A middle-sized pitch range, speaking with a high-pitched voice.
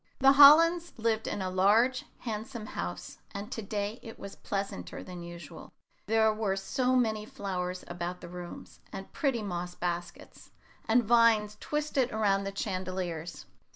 Yes: average, 4.2 semitones; high, 205 Hz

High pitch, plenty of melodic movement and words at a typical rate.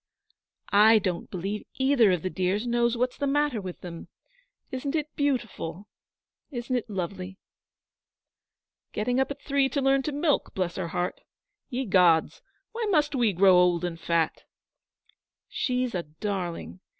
Yes: high, 215 Hz; wide, 6.7 semitones; average, 150 wpm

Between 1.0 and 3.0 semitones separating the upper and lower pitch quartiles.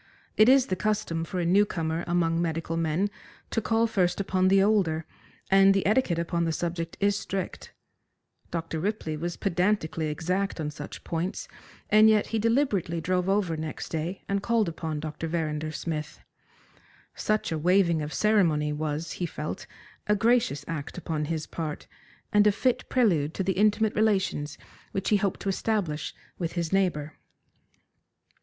No: average, 4.1 semitones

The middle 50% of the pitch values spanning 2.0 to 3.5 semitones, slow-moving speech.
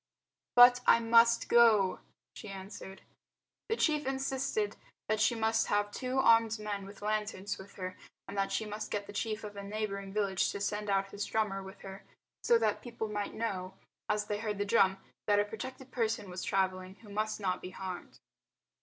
No: narrow, 2.5 semitones; average, 190 wpm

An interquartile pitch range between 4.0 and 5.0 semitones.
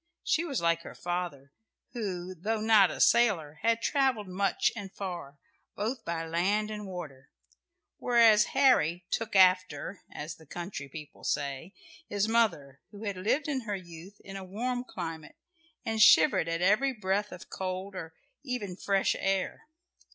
Yes: average, 4.5 semitones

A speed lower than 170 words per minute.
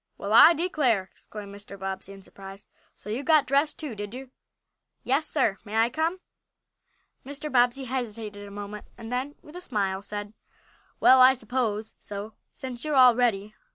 No: average, 175 wpm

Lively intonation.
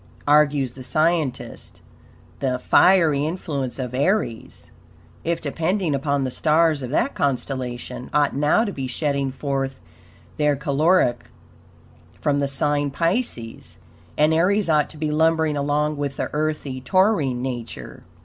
No: average, 3.0 semitones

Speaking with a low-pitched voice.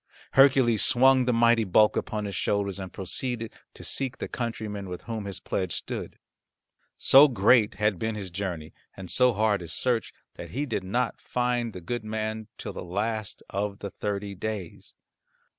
Yes: low, 110 Hz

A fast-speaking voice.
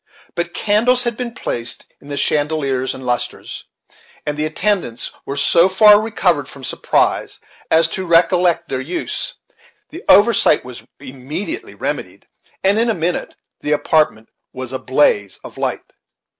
No: average, 150 wpm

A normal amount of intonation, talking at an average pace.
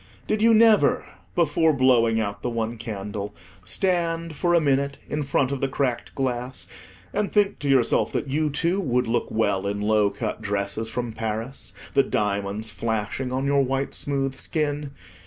Yes: average, 5.0 semitones; average, 170 wpm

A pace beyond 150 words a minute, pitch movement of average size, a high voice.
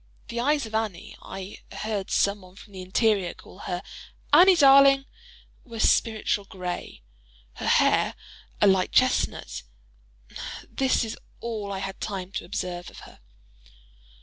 No: average, 140 wpm; average, 3.9 semitones; high, 205 Hz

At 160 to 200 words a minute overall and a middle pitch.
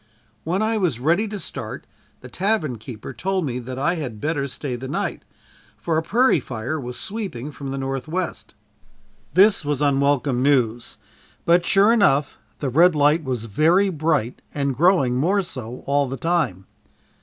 Yes: average, 165 wpm; medium, 145 Hz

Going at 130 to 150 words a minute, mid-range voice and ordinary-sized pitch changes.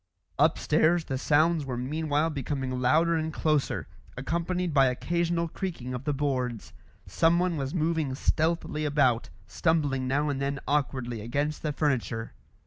Yes: slow, 135 wpm; medium, 145 Hz; average, 3.6 semitones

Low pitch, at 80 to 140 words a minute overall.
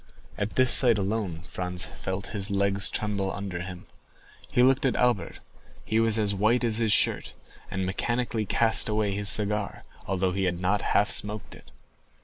No: low, 105 Hz; average, 165 wpm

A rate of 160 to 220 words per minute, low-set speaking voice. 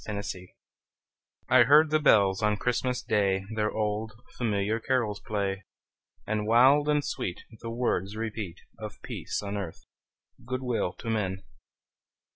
No: average, 140 wpm; low, 110 Hz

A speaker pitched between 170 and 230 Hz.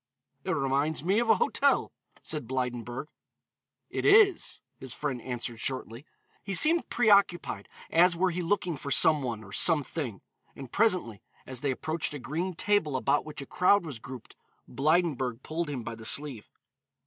No: medium, 145 Hz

